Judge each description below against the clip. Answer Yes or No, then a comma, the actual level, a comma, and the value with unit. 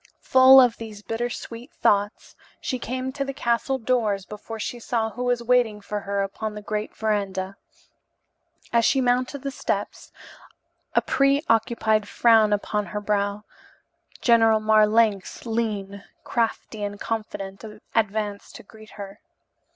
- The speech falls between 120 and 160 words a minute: Yes, average, 140 wpm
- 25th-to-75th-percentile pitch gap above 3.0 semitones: No, average, 2.7 semitones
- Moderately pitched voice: No, high, 220 Hz